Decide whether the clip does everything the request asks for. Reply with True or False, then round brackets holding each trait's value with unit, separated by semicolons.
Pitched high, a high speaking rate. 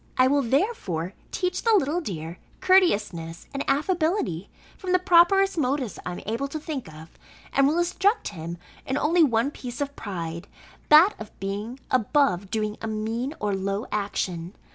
False (250 Hz; 165 wpm)